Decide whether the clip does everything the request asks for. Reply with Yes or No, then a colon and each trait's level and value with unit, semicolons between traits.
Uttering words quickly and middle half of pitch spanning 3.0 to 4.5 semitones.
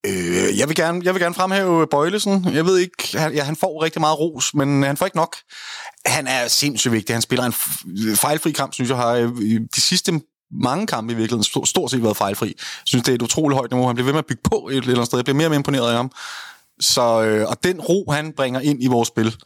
No: fast, 250 wpm; average, 5.2 semitones